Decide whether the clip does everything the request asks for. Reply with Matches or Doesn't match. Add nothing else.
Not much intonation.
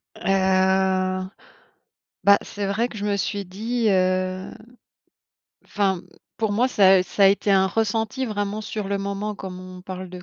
Matches